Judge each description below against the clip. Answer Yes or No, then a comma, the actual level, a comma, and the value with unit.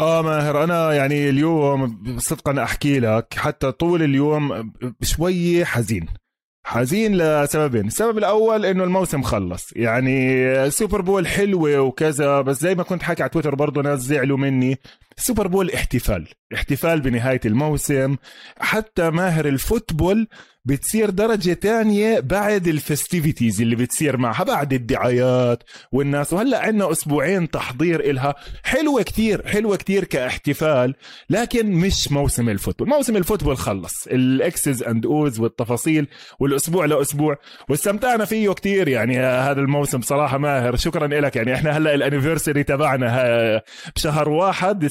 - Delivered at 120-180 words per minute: Yes, average, 130 wpm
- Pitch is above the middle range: No, medium, 145 Hz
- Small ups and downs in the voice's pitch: No, average, 5.3 semitones